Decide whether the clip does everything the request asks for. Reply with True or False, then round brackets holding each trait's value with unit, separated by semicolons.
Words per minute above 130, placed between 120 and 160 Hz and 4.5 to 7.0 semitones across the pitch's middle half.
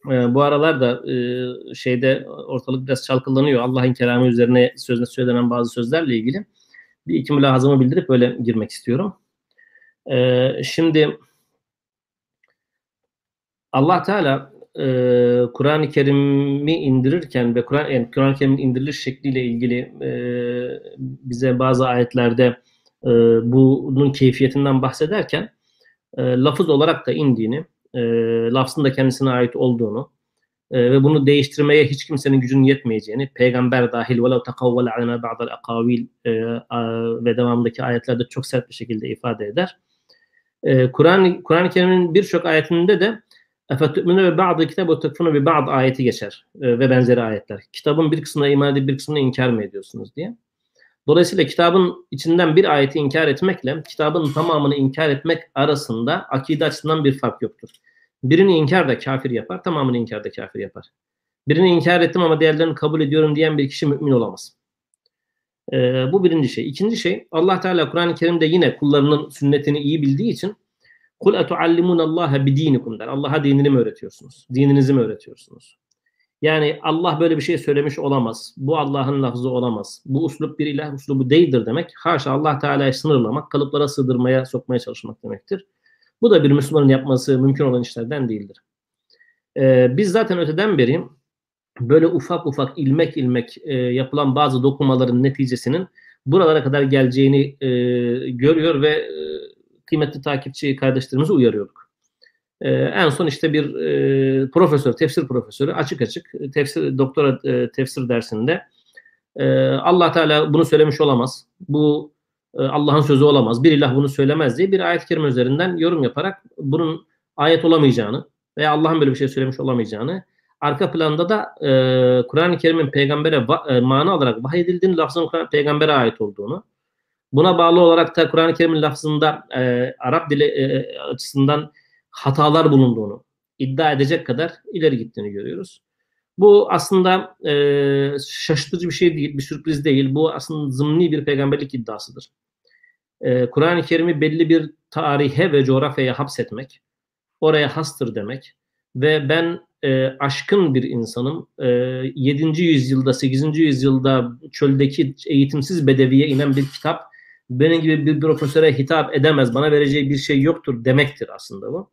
False (140 wpm; 140 Hz; 4.0 semitones)